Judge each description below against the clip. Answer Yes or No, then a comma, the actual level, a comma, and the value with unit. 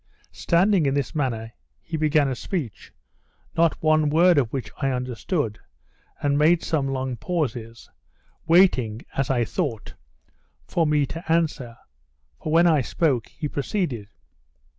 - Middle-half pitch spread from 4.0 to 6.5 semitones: Yes, average, 4.7 semitones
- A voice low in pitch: No, medium, 145 Hz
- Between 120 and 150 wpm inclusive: Yes, average, 140 wpm